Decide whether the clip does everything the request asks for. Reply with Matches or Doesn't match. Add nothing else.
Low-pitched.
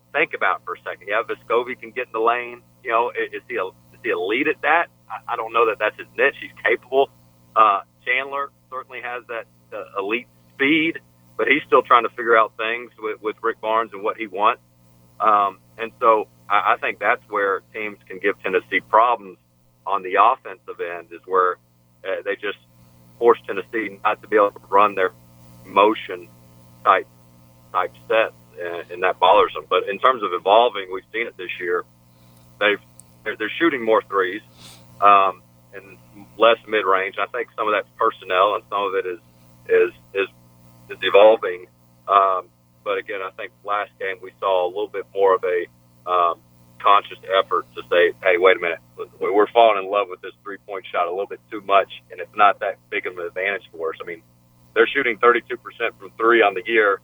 Matches